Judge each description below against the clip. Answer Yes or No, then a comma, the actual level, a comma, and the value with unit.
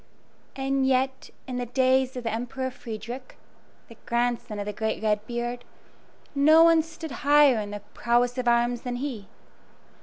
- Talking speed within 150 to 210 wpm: Yes, average, 160 wpm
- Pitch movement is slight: Yes, narrow, 2.2 semitones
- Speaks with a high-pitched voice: Yes, high, 245 Hz